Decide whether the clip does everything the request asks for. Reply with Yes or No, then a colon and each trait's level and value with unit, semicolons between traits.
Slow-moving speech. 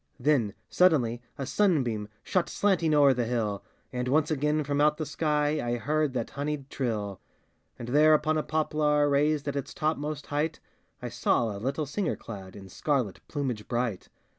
No: average, 170 wpm